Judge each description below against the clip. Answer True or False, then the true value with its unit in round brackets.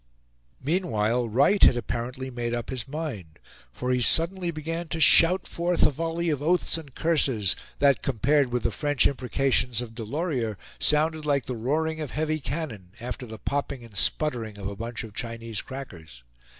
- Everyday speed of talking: True (170 wpm)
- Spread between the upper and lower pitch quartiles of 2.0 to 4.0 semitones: False (5.2 semitones)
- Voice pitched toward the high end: False (130 Hz)